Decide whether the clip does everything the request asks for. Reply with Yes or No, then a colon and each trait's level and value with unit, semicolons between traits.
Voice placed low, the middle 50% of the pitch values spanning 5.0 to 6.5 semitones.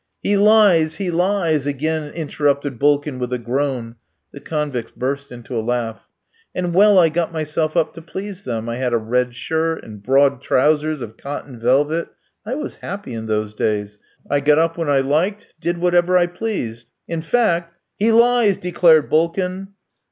No: medium, 155 Hz; wide, 5.6 semitones